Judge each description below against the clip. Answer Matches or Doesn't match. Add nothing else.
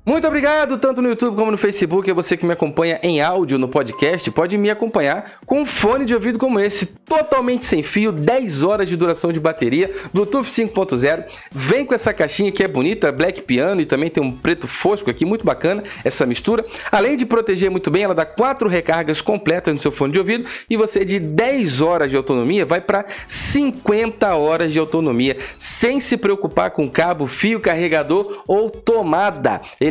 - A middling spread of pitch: Doesn't match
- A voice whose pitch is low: Doesn't match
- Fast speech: Matches